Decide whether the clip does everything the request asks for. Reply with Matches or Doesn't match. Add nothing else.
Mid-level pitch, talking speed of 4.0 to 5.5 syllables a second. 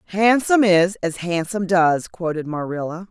Matches